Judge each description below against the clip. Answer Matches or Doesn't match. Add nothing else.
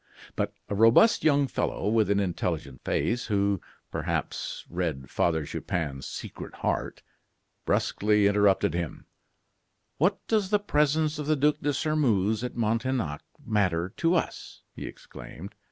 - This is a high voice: Doesn't match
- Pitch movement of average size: Doesn't match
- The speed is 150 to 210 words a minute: Doesn't match